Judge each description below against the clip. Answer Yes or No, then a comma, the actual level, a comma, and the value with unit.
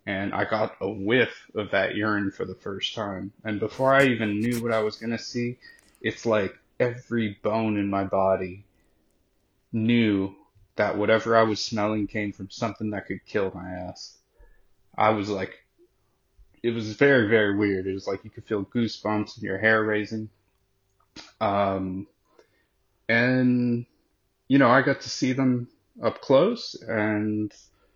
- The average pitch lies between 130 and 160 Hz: No, low, 105 Hz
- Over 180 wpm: No, average, 160 wpm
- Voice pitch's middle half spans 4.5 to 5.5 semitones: No, average, 2.8 semitones